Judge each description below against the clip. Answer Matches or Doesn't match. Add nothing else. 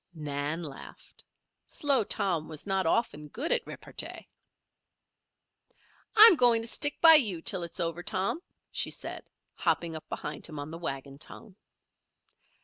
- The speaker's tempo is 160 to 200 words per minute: Doesn't match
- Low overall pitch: Doesn't match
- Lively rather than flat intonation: Matches